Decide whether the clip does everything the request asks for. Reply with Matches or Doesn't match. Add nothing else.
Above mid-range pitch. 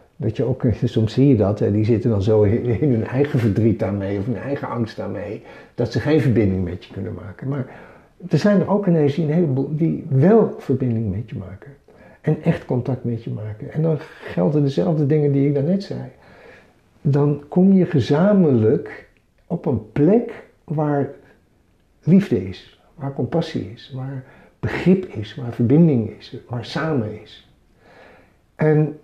Doesn't match